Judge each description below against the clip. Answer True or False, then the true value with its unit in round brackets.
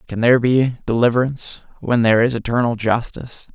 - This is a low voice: True (120 Hz)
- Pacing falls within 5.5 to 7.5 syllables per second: True (6.2 syllables/s)